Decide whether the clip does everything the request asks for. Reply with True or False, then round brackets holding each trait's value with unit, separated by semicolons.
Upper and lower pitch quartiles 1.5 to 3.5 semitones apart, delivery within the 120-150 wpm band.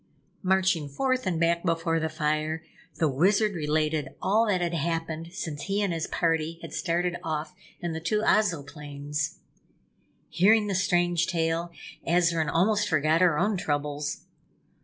True (3.0 semitones; 145 wpm)